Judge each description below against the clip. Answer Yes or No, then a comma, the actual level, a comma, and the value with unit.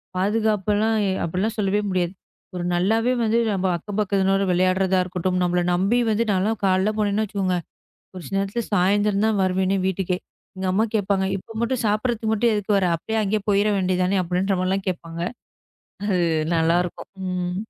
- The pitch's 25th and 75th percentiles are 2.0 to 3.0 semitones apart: Yes, narrow, 2.4 semitones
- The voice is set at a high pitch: Yes, high, 195 Hz